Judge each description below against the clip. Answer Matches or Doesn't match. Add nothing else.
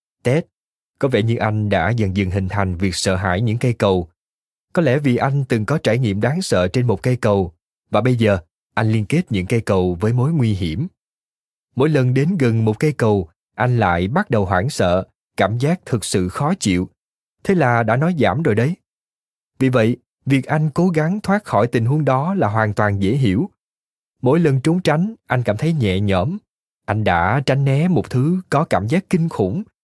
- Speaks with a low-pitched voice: Matches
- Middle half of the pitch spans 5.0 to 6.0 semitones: Doesn't match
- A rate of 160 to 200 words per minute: Doesn't match